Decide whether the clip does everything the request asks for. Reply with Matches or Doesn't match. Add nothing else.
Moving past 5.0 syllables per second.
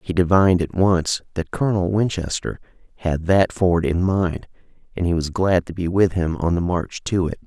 Doesn't match